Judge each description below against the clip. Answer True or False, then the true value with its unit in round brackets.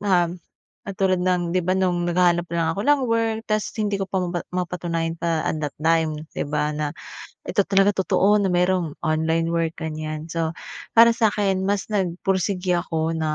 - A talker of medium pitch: True (180 Hz)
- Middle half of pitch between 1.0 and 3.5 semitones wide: True (2.9 semitones)